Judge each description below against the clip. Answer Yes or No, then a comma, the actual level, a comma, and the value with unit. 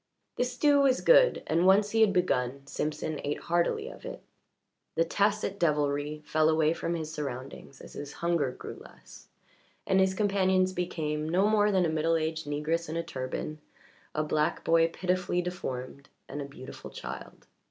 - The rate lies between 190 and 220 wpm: No, average, 170 wpm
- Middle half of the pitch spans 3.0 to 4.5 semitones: Yes, average, 3.8 semitones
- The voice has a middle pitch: Yes, medium, 165 Hz